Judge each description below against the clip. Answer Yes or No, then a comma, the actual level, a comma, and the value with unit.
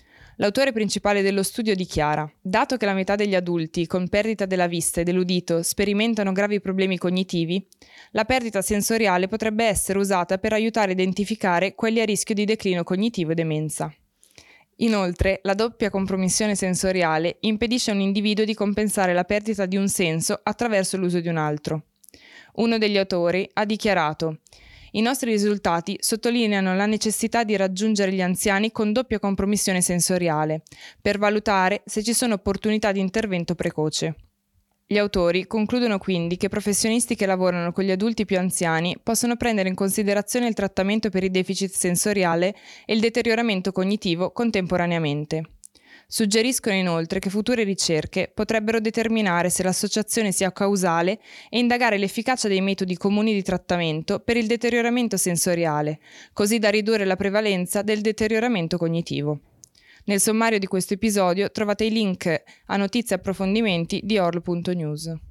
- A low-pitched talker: No, high, 195 Hz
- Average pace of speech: Yes, average, 145 wpm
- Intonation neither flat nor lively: Yes, average, 3.3 semitones